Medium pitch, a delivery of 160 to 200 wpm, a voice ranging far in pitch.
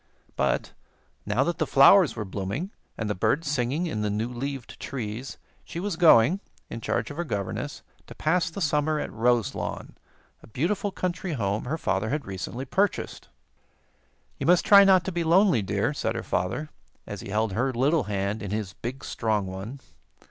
No: low, 130 Hz; average, 180 wpm; wide, 7.5 semitones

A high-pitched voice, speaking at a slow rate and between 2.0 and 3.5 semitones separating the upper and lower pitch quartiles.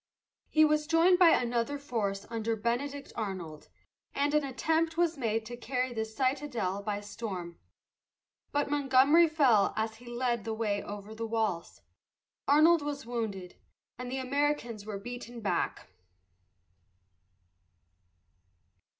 No: high, 240 Hz; slow, 125 wpm; average, 4.8 semitones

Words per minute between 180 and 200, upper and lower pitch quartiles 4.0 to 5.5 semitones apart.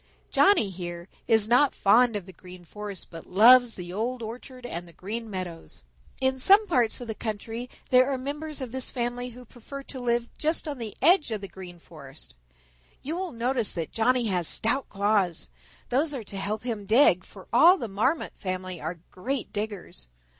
Yes: average, 190 wpm; average, 5.1 semitones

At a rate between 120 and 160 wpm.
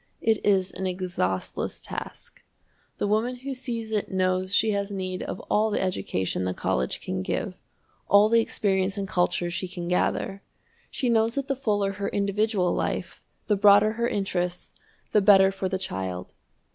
No: average, 170 wpm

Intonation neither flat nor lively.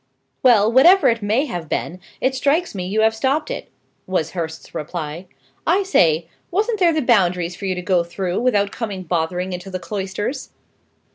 No: wide, 6.5 semitones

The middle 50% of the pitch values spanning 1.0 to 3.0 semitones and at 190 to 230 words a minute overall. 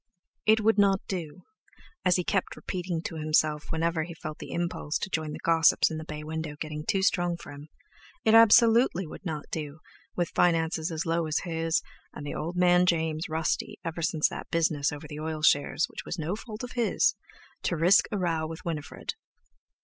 Yes: narrow, 2.6 semitones; average, 195 wpm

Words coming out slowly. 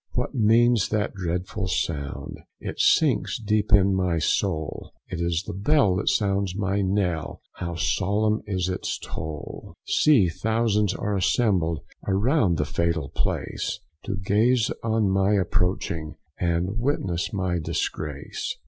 Yes: slow, 130 wpm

